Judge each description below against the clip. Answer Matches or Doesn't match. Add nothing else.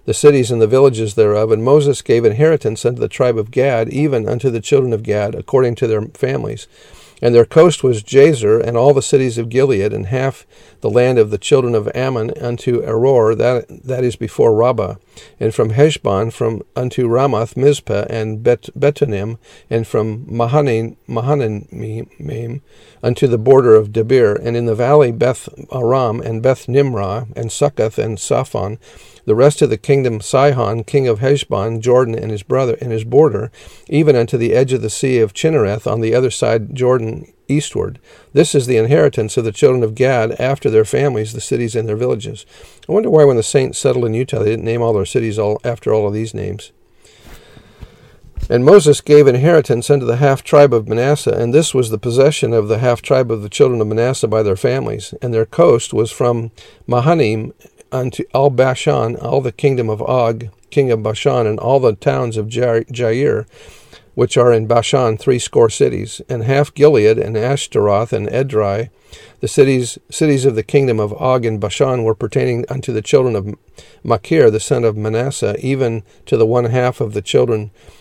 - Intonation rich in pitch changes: Doesn't match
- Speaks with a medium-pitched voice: Doesn't match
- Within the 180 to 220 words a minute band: Matches